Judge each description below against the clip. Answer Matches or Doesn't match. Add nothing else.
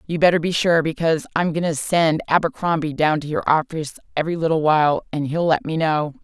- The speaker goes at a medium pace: Doesn't match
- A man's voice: Doesn't match